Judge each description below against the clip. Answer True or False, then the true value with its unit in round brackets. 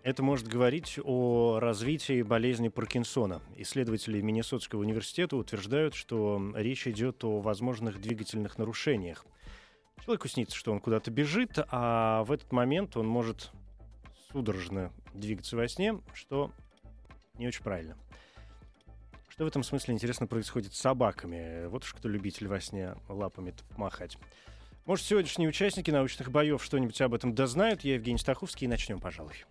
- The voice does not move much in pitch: False (4.0 semitones)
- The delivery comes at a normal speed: True (140 wpm)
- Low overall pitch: True (120 Hz)